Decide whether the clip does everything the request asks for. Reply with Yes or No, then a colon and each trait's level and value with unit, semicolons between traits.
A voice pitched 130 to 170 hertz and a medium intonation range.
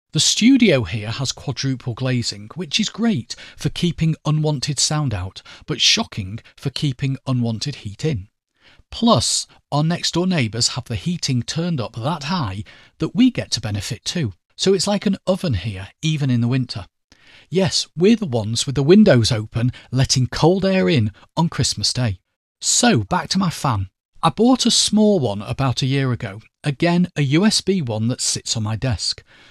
No: low, 135 Hz; wide, 6.8 semitones